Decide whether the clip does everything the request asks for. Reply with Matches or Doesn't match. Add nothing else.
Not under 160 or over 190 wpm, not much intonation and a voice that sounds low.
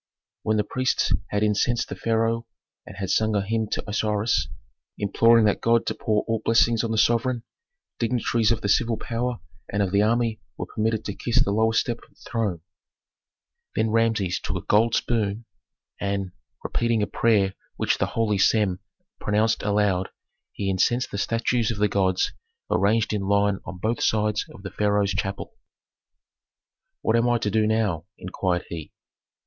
Matches